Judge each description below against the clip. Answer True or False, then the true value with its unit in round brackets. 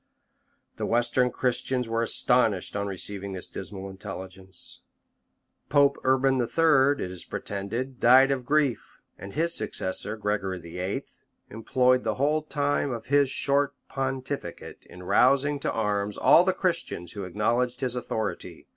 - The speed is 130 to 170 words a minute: True (140 wpm)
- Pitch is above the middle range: False (120 Hz)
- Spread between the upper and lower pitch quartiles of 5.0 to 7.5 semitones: True (5.3 semitones)